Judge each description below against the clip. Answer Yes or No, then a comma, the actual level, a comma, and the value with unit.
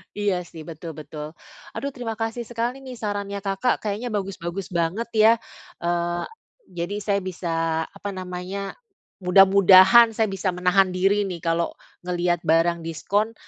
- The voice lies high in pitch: Yes, high, 195 Hz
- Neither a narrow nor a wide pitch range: Yes, average, 3.2 semitones